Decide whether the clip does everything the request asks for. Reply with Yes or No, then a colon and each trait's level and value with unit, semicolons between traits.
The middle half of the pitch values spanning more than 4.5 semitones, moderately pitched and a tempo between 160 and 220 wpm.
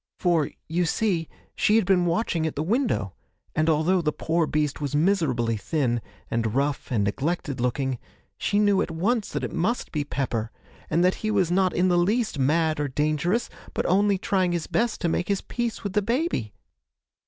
Yes: average, 5.2 semitones; medium, 170 Hz; average, 190 wpm